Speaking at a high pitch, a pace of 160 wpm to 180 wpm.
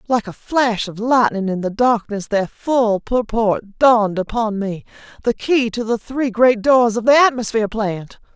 Yes: high, 225 Hz; average, 170 wpm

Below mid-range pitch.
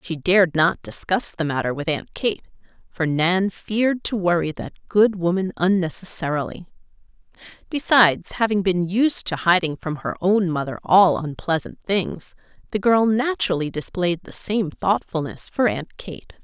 No: medium, 185 Hz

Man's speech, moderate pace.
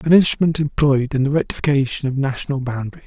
Yes: male; average, 175 wpm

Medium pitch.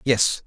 No: low, 115 Hz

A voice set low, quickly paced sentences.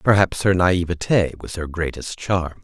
No: very low, 90 Hz; average, 160 wpm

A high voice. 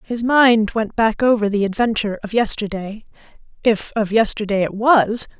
Yes: high, 220 Hz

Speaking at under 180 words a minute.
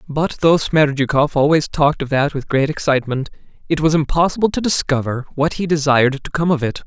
No: average, 190 wpm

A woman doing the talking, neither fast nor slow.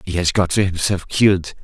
No: male; average, 185 wpm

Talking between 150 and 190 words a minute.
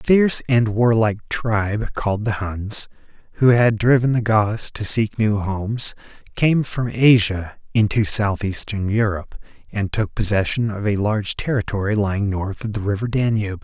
Yes: average, 160 wpm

